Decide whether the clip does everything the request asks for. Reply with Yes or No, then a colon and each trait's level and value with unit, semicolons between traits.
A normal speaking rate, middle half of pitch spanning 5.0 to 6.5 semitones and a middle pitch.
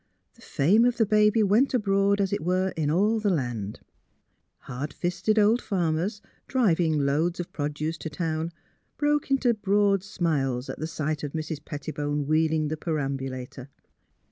Yes: average, 155 wpm; wide, 5.5 semitones; medium, 165 Hz